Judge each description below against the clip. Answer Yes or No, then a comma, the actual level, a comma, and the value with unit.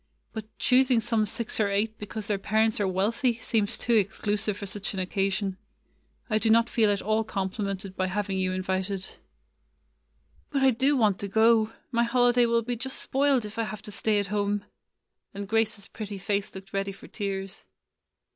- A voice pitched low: No, high, 210 Hz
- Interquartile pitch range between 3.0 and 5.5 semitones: No, narrow, 2.5 semitones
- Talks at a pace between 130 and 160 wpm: No, average, 185 wpm